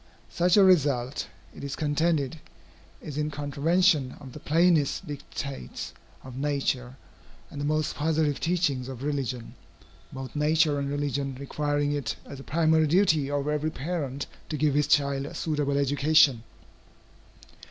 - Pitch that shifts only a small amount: Yes, narrow, 2.1 semitones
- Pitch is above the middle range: No, medium, 145 Hz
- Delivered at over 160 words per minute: No, average, 140 wpm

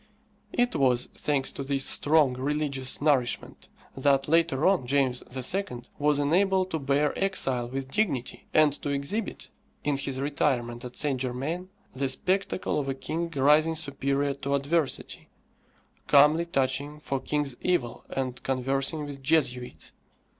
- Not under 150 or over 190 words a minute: No, average, 140 wpm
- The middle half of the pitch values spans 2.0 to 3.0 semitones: Yes, average, 2.7 semitones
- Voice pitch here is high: No, medium, 140 Hz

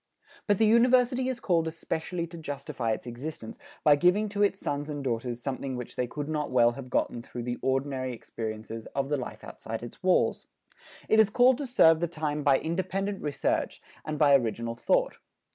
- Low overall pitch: No, medium, 145 Hz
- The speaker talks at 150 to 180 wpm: No, average, 190 wpm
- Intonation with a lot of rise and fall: Yes, wide, 6.8 semitones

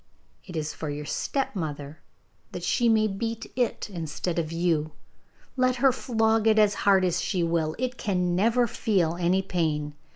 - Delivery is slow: No, average, 165 wpm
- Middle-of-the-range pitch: Yes, medium, 180 Hz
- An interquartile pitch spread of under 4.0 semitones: No, wide, 5.5 semitones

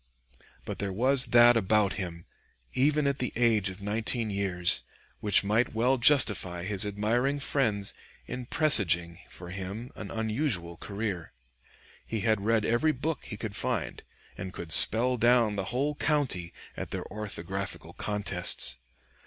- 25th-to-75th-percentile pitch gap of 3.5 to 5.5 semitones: Yes, average, 4.3 semitones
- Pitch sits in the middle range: No, low, 110 Hz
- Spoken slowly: No, average, 145 wpm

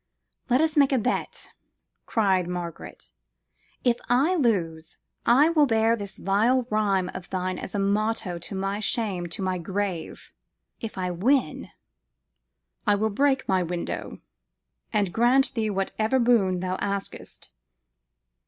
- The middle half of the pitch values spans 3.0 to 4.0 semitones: No, average, 4.5 semitones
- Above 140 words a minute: No, slow, 135 wpm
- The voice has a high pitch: Yes, high, 205 Hz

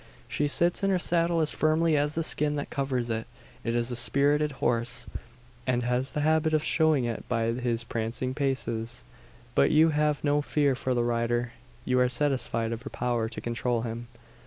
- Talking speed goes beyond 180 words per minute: Yes, average, 190 wpm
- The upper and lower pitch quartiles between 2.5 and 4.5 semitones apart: Yes, average, 4.0 semitones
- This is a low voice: Yes, low, 130 Hz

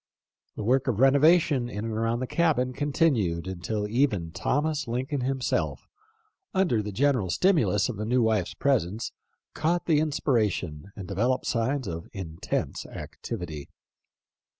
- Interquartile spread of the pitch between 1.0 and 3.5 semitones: No, wide, 5.6 semitones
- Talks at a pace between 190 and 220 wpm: No, slow, 135 wpm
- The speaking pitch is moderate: No, low, 120 Hz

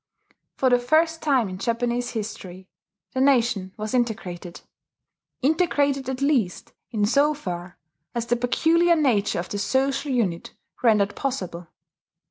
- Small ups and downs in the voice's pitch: No, wide, 5.5 semitones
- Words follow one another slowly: Yes, slow, 130 wpm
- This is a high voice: Yes, high, 245 Hz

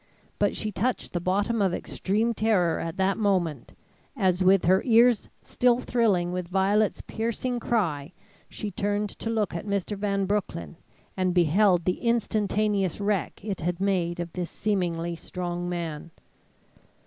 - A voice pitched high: Yes, high, 195 Hz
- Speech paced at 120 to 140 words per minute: No, average, 150 wpm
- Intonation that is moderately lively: Yes, average, 3.3 semitones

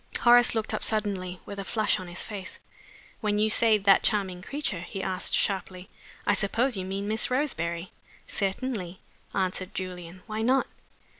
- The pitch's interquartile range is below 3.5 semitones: Yes, average, 2.9 semitones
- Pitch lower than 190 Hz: No, high, 195 Hz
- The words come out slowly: No, average, 160 wpm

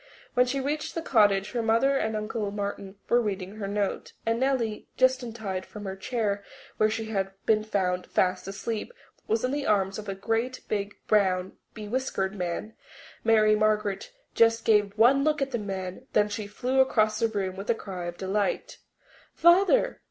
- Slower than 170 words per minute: No, average, 180 wpm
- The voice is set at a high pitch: Yes, high, 215 Hz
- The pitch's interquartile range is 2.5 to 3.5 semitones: Yes, average, 3.2 semitones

